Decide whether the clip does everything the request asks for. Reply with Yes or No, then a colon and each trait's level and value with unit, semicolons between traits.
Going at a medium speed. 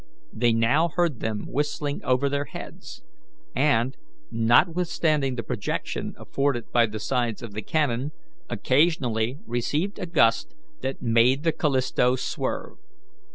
No: slow, 125 wpm